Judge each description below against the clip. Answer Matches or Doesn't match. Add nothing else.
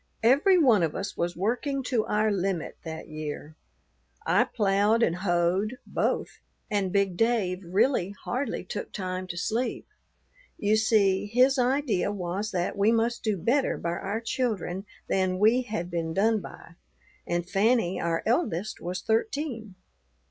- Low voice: Doesn't match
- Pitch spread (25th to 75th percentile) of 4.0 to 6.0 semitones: Matches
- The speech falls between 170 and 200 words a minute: Doesn't match